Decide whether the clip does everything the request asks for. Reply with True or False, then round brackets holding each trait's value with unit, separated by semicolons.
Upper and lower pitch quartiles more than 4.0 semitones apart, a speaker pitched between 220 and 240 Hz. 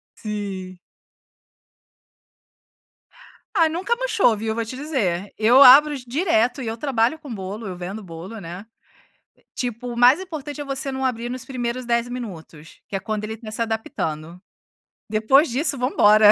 True (4.4 semitones; 235 Hz)